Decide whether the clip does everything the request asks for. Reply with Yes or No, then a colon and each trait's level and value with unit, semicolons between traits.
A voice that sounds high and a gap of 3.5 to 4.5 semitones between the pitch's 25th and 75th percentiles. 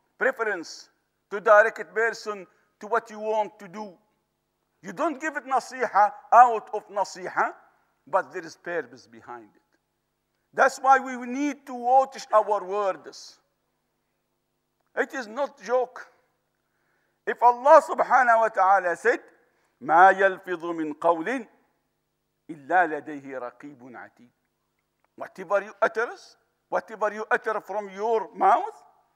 No: high, 210 Hz; average, 4.9 semitones